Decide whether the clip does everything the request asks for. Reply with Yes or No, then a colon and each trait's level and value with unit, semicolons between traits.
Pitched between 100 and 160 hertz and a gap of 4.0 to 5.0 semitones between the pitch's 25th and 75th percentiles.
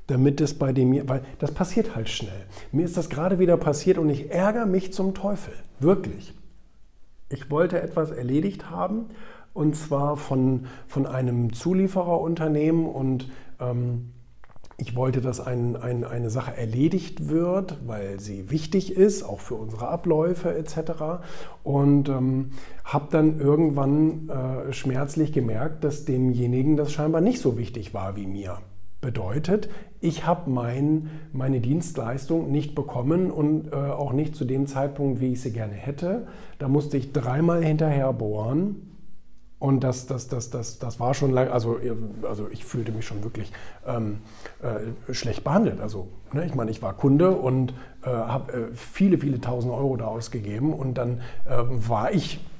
Yes: low, 135 Hz; average, 4.6 semitones